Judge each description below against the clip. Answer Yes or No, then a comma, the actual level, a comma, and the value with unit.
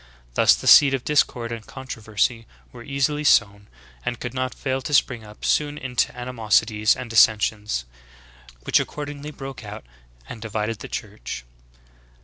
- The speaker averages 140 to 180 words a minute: Yes, average, 160 wpm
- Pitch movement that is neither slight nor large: Yes, average, 3.7 semitones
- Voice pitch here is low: Yes, low, 120 Hz